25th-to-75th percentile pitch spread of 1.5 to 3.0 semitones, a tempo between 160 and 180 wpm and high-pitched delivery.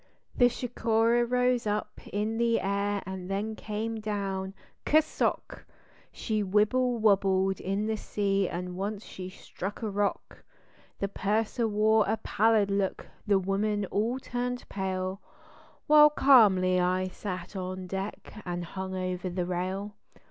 No: average, 2.7 semitones; average, 140 wpm; high, 205 Hz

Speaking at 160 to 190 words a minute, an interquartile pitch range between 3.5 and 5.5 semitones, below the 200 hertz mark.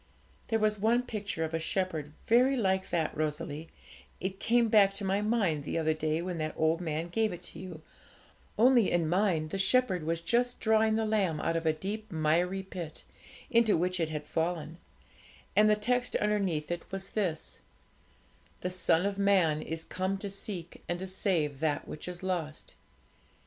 Yes: average, 180 wpm; average, 4.6 semitones; medium, 185 Hz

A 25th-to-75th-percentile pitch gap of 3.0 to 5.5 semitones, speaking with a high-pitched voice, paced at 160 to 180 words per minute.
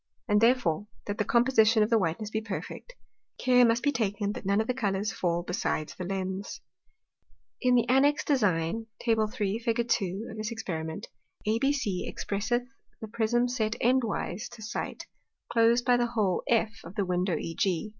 Yes: average, 3.6 semitones; high, 220 Hz; average, 170 wpm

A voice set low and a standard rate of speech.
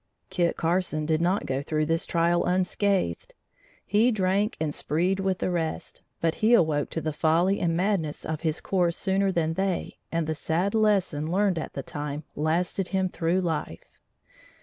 No: medium, 170 Hz; average, 170 wpm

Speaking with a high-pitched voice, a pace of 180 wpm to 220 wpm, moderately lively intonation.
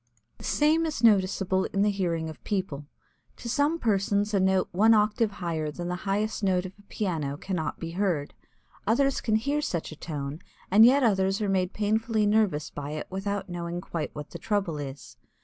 Yes: high, 195 Hz; average, 190 wpm; average, 4.2 semitones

